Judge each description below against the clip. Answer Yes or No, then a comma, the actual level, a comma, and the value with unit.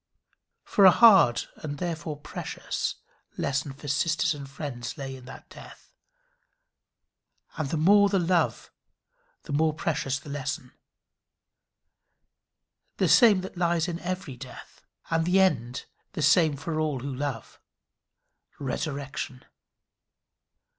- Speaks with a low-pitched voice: No, medium, 150 Hz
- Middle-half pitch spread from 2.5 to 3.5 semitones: No, average, 4.0 semitones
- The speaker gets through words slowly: Yes, slow, 120 wpm